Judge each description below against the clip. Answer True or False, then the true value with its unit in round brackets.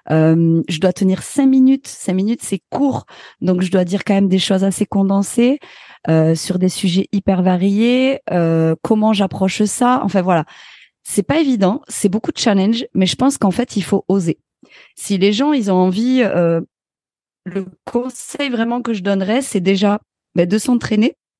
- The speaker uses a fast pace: False (180 wpm)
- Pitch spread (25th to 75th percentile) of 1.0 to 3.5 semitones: False (4.4 semitones)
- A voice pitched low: False (200 Hz)